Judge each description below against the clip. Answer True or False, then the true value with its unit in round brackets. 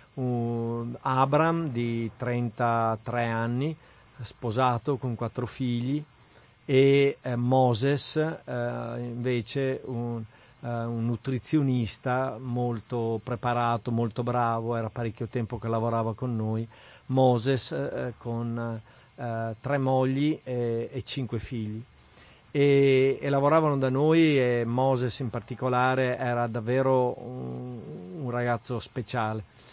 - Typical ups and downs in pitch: False (2.1 semitones)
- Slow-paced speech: True (105 wpm)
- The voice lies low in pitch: True (120 Hz)